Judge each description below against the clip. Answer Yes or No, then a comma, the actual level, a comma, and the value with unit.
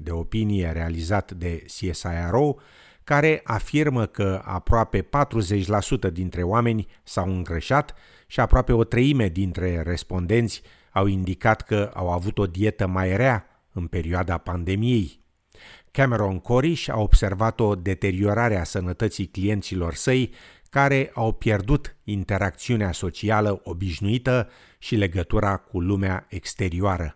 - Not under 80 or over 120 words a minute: Yes, slow, 115 wpm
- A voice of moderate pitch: No, low, 100 Hz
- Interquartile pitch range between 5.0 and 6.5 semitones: No, average, 3.9 semitones